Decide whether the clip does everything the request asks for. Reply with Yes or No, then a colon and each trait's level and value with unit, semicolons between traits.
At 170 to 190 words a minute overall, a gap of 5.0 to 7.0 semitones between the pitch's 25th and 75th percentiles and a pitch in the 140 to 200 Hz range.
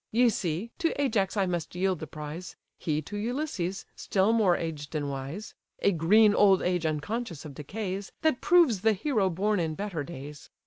Yes: average, 180 wpm; average, 5.3 semitones; high, 190 Hz